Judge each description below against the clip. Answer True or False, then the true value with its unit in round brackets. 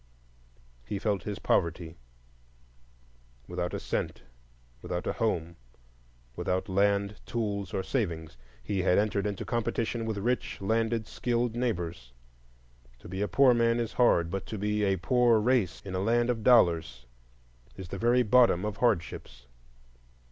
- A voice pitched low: True (105 Hz)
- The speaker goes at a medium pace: True (145 wpm)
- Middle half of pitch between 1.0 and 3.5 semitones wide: False (4.2 semitones)